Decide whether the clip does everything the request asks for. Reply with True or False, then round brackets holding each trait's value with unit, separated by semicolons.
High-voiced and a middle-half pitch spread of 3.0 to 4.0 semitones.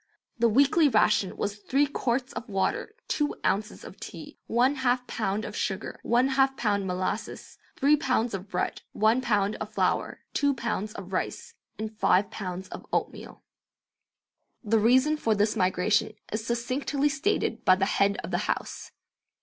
False (225 Hz; 4.5 semitones)